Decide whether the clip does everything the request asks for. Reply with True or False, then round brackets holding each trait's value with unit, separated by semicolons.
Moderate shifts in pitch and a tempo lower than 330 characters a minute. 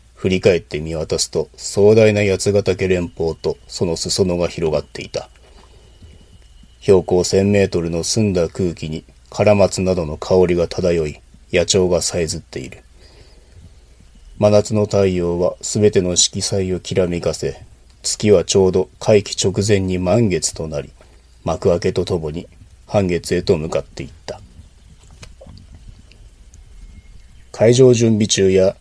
True (3.3 semitones; 245 characters per minute)